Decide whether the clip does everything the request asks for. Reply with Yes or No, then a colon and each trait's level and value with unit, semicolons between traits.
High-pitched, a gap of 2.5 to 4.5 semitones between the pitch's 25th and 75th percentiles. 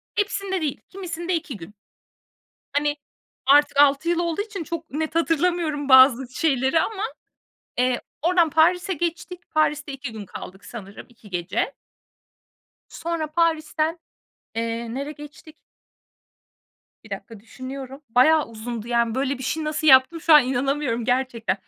No: very high, 290 Hz; average, 5.0 semitones